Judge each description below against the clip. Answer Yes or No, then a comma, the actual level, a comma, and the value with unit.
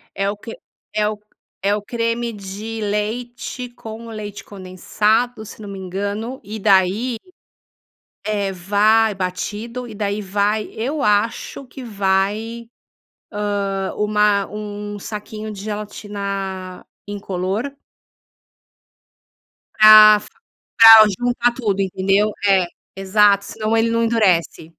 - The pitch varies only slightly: Yes, narrow, 2.1 semitones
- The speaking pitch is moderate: No, high, 210 Hz